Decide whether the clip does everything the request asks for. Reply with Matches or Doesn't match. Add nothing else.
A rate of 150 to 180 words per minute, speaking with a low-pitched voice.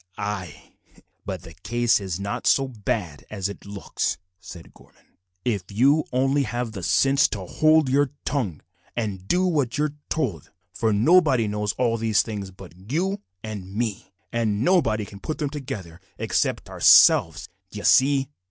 Matches